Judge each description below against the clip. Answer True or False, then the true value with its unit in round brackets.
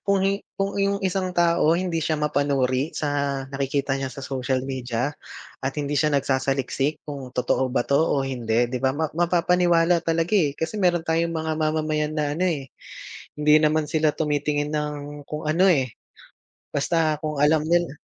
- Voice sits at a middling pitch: True (150 Hz)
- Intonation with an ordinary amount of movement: True (3.1 semitones)